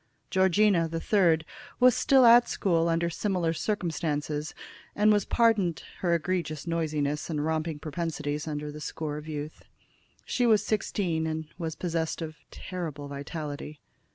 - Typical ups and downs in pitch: Yes, average, 3.4 semitones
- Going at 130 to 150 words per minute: Yes, average, 140 wpm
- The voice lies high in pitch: No, medium, 165 Hz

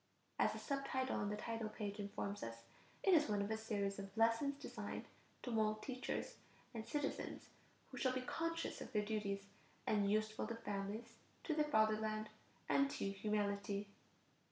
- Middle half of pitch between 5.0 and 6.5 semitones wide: No, average, 3.8 semitones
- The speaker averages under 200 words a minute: Yes, average, 170 wpm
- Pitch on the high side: Yes, high, 215 Hz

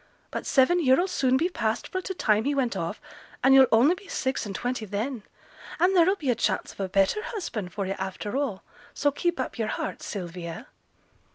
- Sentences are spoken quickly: Yes, fast, 210 wpm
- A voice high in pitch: Yes, very high, 260 Hz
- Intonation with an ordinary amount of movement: No, wide, 8.0 semitones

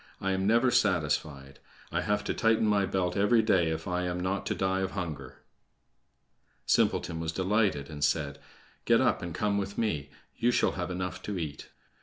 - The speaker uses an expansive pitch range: No, average, 4.1 semitones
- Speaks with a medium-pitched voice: No, very low, 90 Hz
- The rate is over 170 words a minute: Yes, average, 185 wpm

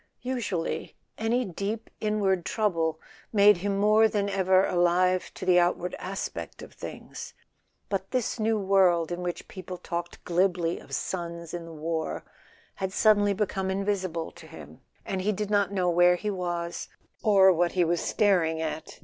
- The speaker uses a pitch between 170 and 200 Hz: Yes, medium, 185 Hz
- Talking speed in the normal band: Yes, average, 160 wpm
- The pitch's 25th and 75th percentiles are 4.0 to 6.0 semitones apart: No, average, 2.7 semitones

